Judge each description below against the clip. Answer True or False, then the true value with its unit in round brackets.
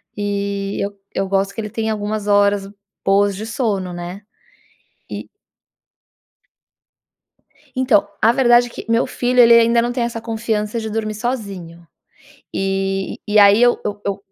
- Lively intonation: False (2.7 semitones)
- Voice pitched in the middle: False (210 Hz)